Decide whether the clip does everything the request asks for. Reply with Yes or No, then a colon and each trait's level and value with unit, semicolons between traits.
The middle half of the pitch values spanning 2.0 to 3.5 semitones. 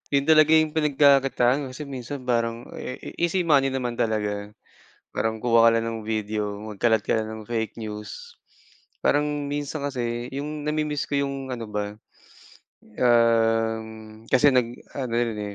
No: average, 4.1 semitones